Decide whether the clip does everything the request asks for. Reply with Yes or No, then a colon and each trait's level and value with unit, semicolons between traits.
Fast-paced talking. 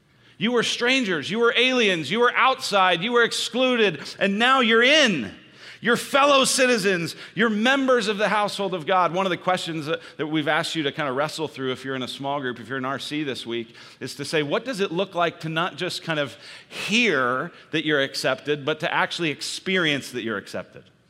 Yes: fast, 215 wpm